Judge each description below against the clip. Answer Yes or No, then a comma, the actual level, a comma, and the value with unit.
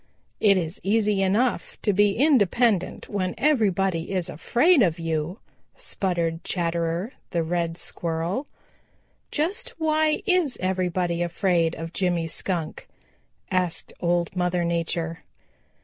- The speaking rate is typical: No, slow, 115 wpm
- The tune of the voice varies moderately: Yes, average, 4.0 semitones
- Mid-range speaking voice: Yes, medium, 180 Hz